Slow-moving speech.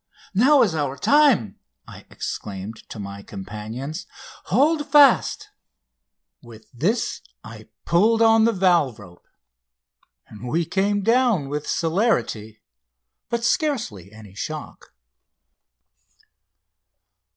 Yes: slow, 100 wpm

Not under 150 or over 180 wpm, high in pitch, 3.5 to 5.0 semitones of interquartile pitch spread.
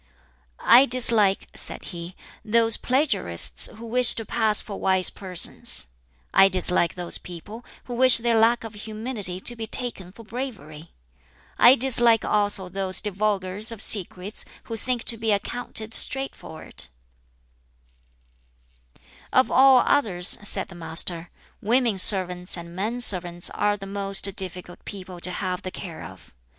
No: average, 140 wpm; high, 205 Hz; average, 4.2 semitones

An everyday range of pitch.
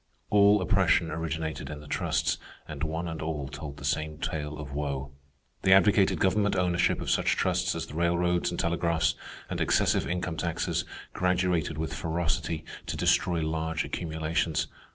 No: narrow, 2.3 semitones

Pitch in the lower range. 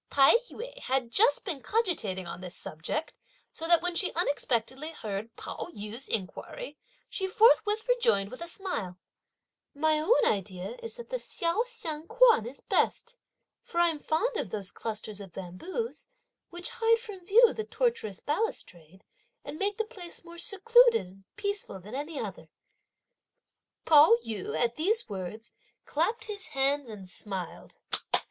No: very high, 315 Hz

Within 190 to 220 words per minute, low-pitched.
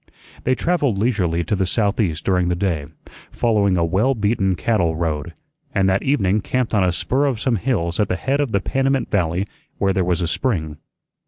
Yes: average, 195 wpm; low, 100 Hz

